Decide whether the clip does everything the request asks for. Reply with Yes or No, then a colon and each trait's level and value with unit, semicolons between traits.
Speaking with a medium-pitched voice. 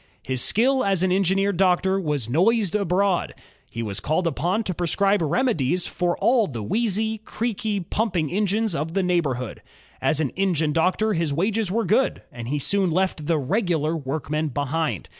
Yes: medium, 180 Hz